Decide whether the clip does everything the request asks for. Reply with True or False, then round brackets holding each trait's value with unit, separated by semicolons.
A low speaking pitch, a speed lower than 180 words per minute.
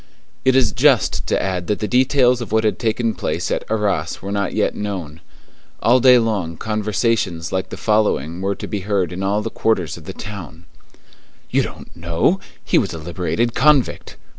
False (105 Hz; 185 wpm)